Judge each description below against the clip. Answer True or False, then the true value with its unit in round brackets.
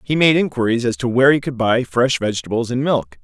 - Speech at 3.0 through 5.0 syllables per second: False (6.1 syllables/s)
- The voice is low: True (125 Hz)